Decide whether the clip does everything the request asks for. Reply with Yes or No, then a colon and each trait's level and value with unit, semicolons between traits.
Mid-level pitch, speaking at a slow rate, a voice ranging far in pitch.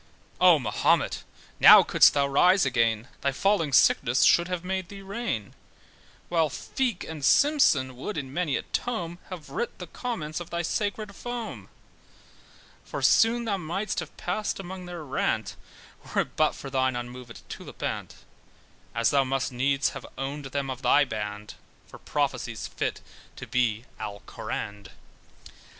No: medium, 150 Hz; average, 145 wpm; wide, 6.7 semitones